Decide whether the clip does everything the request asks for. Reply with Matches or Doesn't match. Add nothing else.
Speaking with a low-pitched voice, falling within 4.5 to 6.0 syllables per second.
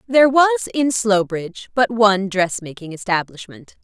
Doesn't match